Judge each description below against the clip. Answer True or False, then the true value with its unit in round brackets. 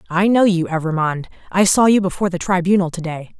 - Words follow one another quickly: True (210 wpm)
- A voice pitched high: False (180 Hz)